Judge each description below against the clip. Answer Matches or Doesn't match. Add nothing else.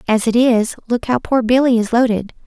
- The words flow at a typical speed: Doesn't match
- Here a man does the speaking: Doesn't match